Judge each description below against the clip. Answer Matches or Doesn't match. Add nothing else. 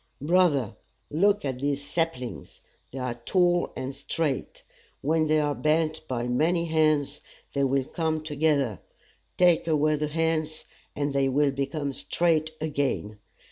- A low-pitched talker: Doesn't match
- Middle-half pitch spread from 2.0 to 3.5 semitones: Matches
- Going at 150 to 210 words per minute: Doesn't match